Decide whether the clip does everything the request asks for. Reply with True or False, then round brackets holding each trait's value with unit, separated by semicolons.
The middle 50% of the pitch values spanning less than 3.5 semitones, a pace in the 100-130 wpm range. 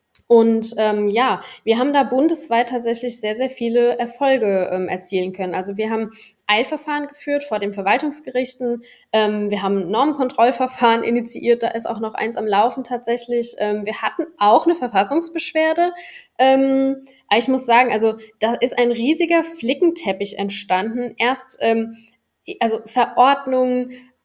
False (3.1 semitones; 140 wpm)